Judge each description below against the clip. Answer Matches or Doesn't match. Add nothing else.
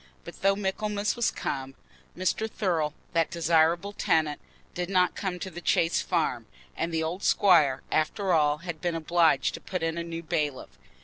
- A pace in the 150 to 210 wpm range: Matches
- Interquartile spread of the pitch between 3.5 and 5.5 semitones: Doesn't match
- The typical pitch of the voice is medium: Matches